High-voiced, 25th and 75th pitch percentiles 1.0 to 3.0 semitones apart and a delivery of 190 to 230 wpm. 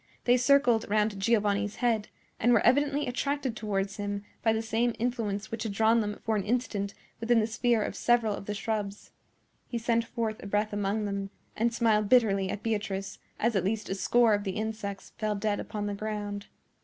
Yes: high, 215 Hz; narrow, 2.4 semitones; average, 195 wpm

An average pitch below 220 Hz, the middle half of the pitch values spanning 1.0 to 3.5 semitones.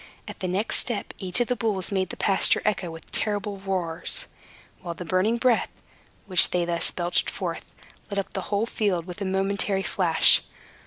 Yes: high, 190 Hz; narrow, 2.4 semitones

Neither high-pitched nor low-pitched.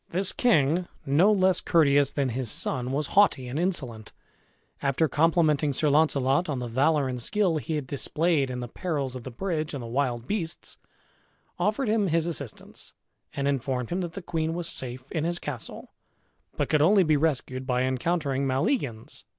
Yes: medium, 145 Hz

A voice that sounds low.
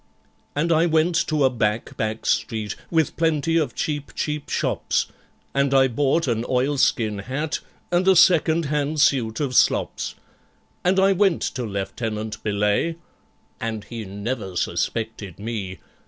Yes: low, 130 Hz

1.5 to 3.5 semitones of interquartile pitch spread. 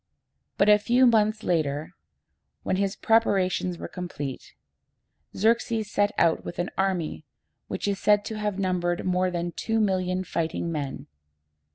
Yes: average, 3.1 semitones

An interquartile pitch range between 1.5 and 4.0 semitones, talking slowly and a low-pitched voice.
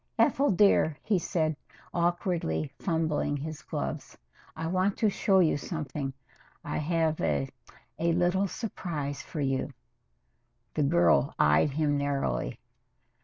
No: average, 3.7 semitones; slow, 120 wpm; medium, 160 Hz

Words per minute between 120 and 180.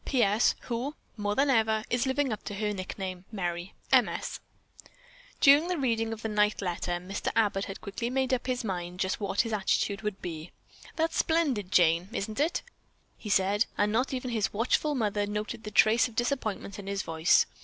No: average, 195 wpm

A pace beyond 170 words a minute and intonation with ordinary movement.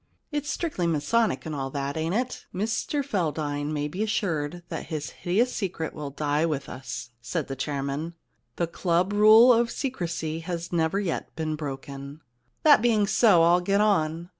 No: average, 185 wpm; wide, 5.8 semitones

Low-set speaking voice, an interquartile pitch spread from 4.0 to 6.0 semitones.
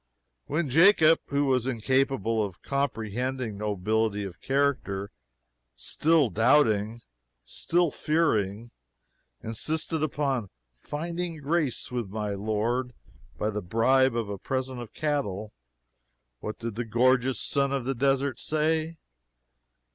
Yes: low, 125 Hz; average, 4.8 semitones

